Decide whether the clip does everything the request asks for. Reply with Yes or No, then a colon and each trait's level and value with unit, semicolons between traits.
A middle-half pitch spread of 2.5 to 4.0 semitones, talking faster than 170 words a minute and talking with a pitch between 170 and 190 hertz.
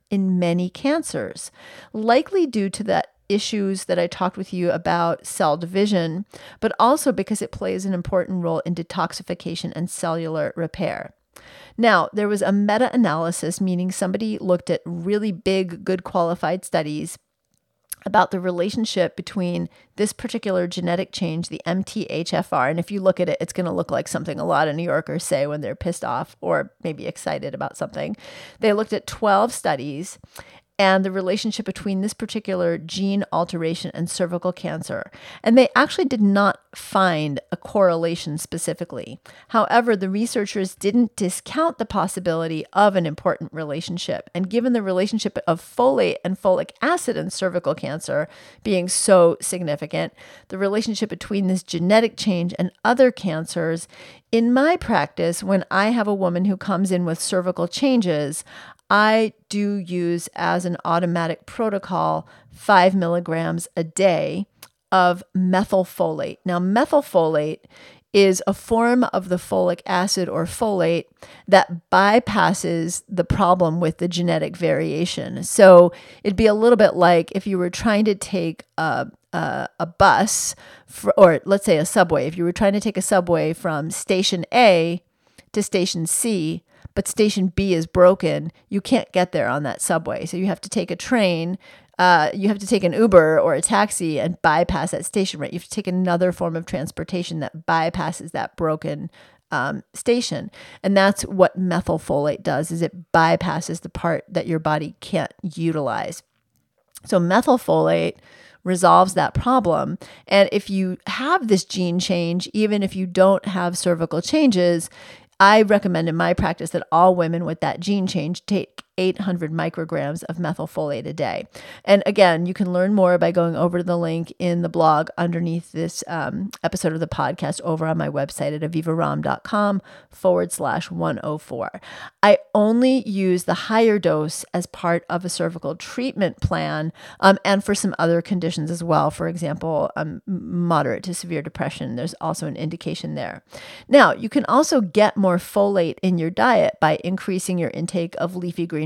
No: average, 3.1 semitones; average, 165 wpm; medium, 185 Hz